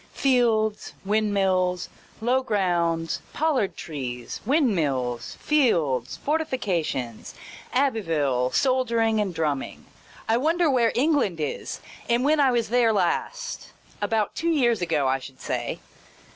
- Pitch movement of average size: No, wide, 7.9 semitones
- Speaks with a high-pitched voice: Yes, high, 215 Hz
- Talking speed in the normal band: No, slow, 115 wpm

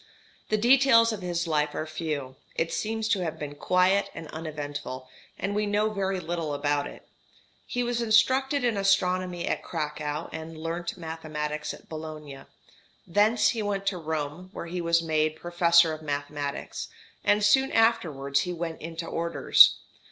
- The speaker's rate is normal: Yes, average, 160 wpm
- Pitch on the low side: No, medium, 170 Hz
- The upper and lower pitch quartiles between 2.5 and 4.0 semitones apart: No, average, 4.8 semitones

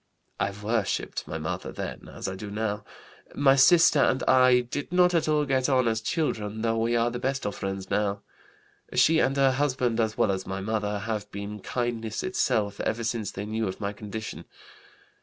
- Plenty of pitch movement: No, average, 4.2 semitones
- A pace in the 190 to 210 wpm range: Yes, average, 195 wpm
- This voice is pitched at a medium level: No, low, 115 Hz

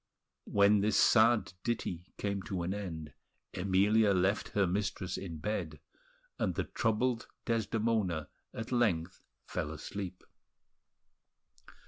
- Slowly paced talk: Yes, slow, 110 wpm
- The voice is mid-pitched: No, low, 100 Hz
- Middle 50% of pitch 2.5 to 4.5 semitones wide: Yes, average, 3.3 semitones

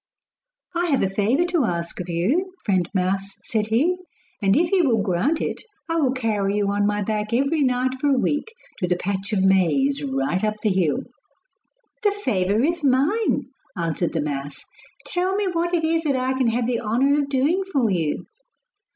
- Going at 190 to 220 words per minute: Yes, average, 195 wpm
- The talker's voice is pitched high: Yes, high, 240 Hz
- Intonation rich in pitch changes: Yes, wide, 7.1 semitones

